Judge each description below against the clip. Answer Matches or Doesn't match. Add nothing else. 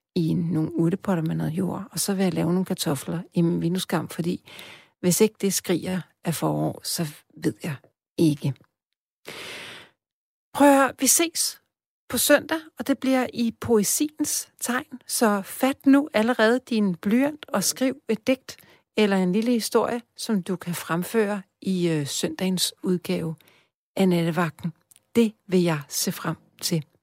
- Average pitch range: Doesn't match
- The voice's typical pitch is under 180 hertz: Doesn't match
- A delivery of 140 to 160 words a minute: Matches